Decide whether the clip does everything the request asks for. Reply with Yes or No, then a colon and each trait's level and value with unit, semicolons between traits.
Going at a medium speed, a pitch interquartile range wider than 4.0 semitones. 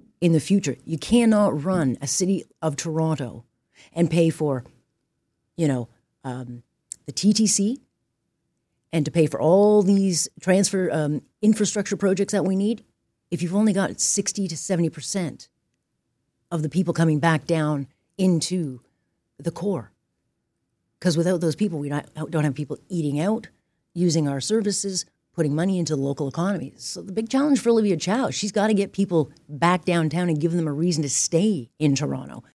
Yes: average, 170 wpm; average, 4.7 semitones